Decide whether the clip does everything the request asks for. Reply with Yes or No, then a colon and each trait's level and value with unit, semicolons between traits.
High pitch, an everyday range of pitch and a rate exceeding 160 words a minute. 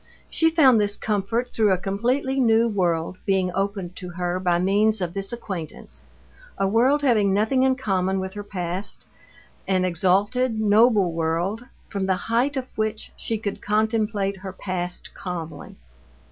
No: high, 200 Hz; average, 3.4 semitones; average, 155 wpm